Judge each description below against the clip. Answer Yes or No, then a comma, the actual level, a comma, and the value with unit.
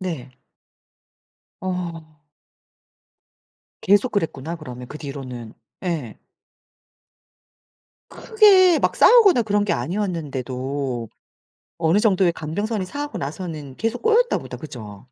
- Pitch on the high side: No, medium, 170 Hz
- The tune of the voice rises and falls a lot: Yes, wide, 7.2 semitones